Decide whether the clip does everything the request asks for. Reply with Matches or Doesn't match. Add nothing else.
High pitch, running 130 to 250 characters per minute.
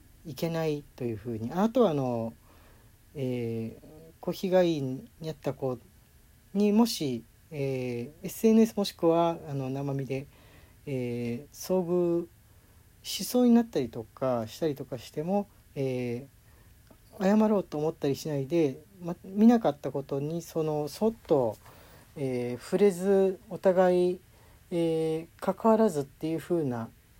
Doesn't match